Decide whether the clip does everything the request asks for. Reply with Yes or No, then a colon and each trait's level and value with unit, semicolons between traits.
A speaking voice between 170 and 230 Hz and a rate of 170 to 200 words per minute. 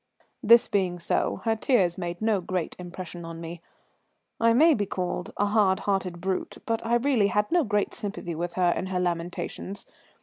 Yes: high, 190 Hz; average, 180 wpm